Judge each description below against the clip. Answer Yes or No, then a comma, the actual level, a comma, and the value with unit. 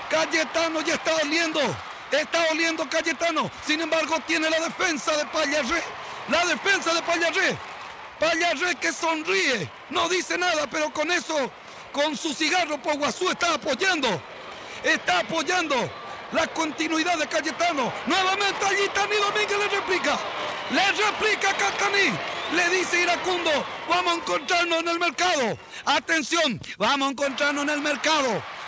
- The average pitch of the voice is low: No, very high, 330 Hz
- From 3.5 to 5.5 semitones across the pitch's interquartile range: No, narrow, 2.4 semitones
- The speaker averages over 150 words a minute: No, average, 135 wpm